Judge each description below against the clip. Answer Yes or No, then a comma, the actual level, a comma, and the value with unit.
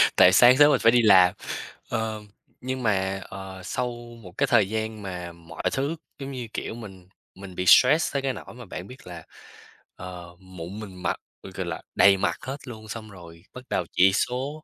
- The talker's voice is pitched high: No, low, 100 Hz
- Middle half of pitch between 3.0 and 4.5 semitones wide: No, average, 5.1 semitones